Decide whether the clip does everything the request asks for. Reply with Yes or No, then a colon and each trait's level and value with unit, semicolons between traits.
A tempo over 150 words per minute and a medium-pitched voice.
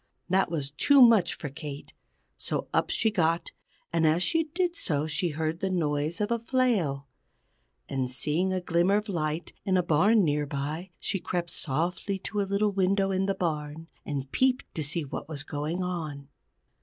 Yes: average, 180 wpm; medium, 170 Hz